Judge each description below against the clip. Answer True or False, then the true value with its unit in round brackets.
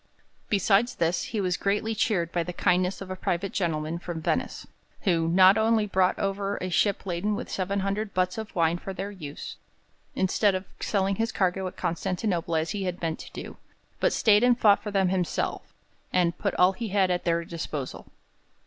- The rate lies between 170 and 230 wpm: True (190 wpm)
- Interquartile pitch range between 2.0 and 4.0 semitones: True (2.6 semitones)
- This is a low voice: False (185 Hz)